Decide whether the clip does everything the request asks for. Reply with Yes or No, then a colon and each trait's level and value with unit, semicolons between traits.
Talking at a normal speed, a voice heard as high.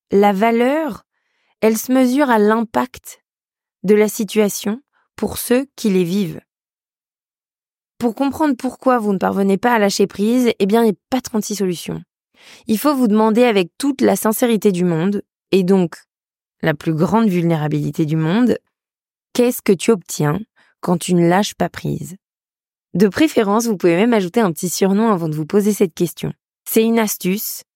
Yes: average, 170 wpm; high, 210 Hz